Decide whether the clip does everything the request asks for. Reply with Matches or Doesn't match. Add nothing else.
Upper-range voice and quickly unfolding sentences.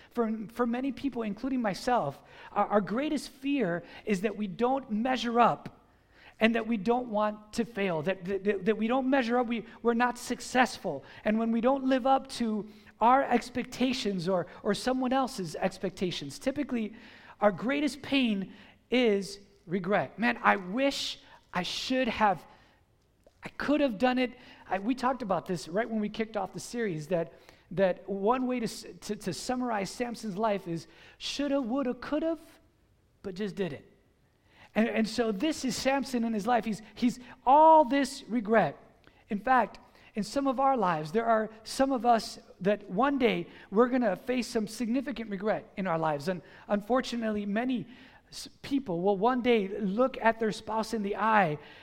Doesn't match